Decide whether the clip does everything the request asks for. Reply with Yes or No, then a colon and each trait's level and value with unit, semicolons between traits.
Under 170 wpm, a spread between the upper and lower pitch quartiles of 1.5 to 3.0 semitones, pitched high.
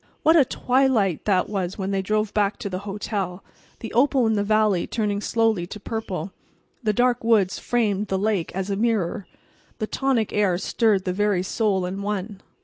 No: average, 185 wpm; narrow, 2.6 semitones; high, 205 Hz